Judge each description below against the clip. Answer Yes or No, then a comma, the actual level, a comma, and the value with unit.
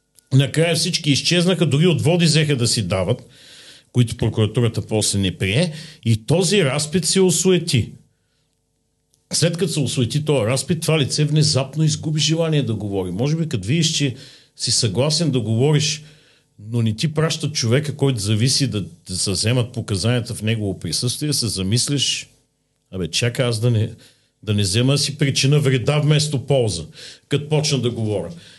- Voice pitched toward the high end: No, low, 135 Hz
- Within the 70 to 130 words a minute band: No, average, 155 wpm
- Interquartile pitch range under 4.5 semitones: No, average, 4.8 semitones